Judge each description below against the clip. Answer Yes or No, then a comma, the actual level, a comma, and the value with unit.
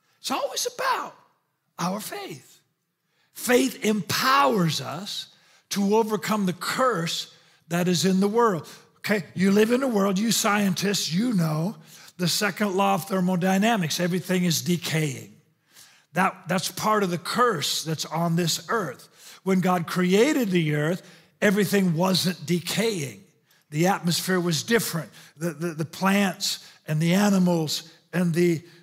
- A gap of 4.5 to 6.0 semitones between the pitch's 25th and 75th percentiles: No, average, 3.5 semitones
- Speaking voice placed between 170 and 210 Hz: Yes, medium, 185 Hz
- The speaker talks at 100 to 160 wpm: Yes, slow, 135 wpm